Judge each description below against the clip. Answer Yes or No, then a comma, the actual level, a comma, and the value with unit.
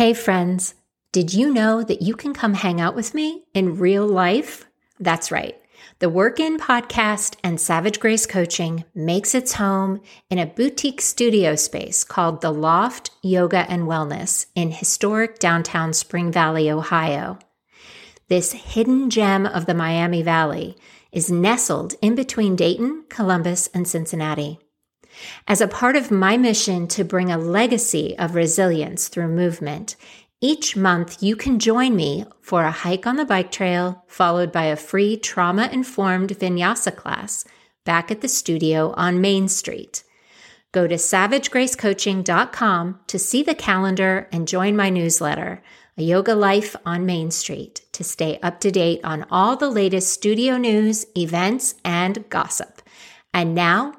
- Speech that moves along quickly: No, average, 150 wpm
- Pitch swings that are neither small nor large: Yes, average, 4.4 semitones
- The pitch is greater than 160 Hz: Yes, high, 190 Hz